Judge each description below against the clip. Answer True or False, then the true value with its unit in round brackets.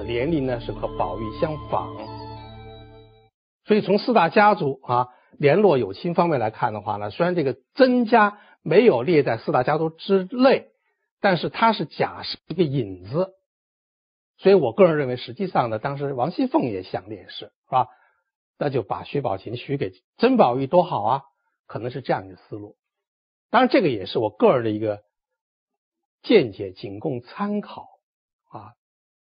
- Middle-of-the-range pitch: True (160 Hz)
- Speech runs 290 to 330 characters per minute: False (245 characters per minute)